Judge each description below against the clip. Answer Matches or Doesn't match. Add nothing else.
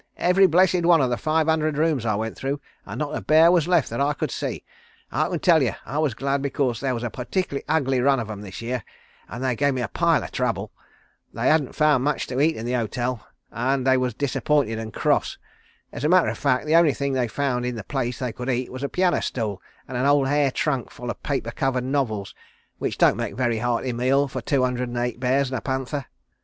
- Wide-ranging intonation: Doesn't match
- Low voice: Matches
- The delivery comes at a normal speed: Doesn't match